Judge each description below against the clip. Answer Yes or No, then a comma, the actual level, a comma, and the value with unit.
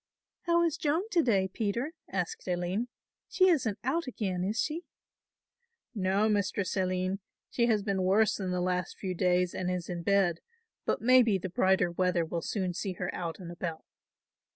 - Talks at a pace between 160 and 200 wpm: Yes, average, 170 wpm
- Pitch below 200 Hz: Yes, high, 190 Hz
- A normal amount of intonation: Yes, average, 3.8 semitones